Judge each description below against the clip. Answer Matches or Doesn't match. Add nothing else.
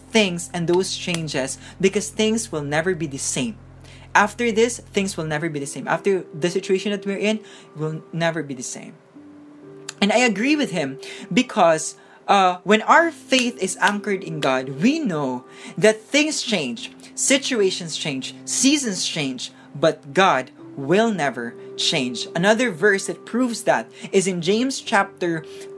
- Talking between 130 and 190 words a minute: Matches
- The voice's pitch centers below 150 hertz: Doesn't match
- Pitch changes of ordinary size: Doesn't match